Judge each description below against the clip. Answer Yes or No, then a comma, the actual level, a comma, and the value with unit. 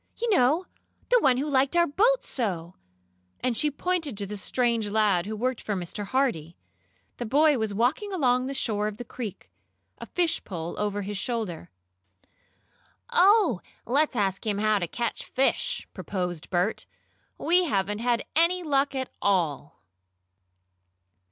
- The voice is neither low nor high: No, high, 240 Hz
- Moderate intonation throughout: No, wide, 6.5 semitones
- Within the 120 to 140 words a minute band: No, average, 150 wpm